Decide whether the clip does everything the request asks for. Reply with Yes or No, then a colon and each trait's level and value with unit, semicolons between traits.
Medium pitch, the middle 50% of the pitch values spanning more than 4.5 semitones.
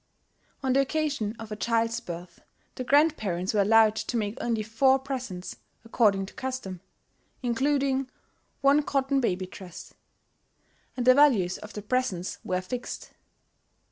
No: high, 230 Hz; average, 5.0 semitones